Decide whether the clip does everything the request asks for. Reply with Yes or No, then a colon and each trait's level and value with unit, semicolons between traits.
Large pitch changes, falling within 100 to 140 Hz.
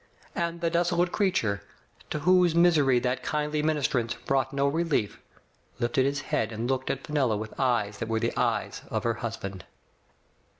Yes: wide, 5.7 semitones; low, 135 Hz